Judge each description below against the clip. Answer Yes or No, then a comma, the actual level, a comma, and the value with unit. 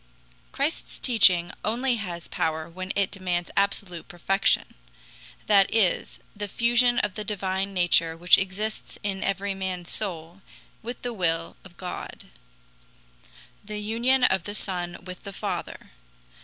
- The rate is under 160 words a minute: Yes, slow, 135 wpm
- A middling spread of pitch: Yes, average, 3.1 semitones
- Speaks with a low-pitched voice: No, high, 195 Hz